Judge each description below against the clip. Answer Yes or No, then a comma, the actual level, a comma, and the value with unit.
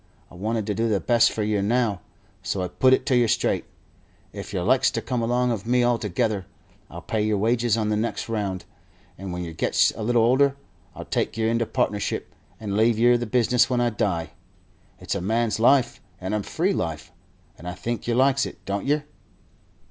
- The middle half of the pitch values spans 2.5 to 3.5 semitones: Yes, average, 3.2 semitones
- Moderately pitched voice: No, low, 115 Hz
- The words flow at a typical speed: No, fast, 210 wpm